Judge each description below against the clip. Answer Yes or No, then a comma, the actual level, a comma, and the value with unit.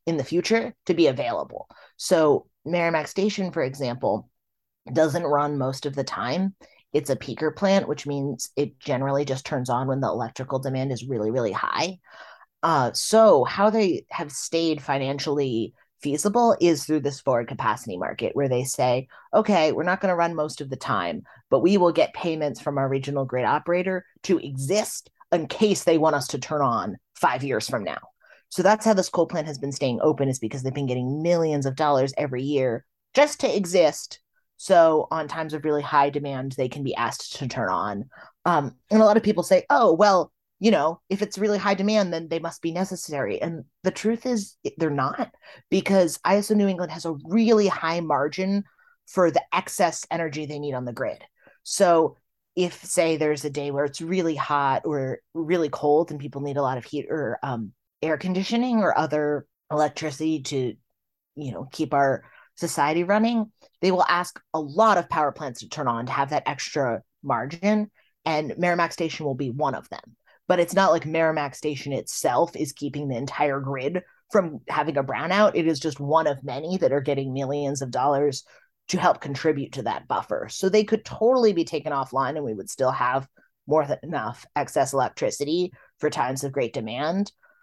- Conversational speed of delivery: Yes, average, 195 wpm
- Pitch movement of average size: Yes, average, 4.7 semitones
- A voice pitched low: No, medium, 155 Hz